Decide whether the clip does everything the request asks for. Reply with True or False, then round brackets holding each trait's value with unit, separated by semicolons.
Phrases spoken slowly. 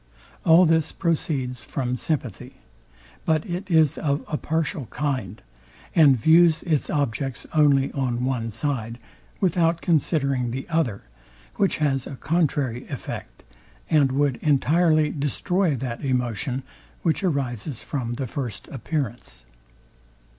True (120 wpm)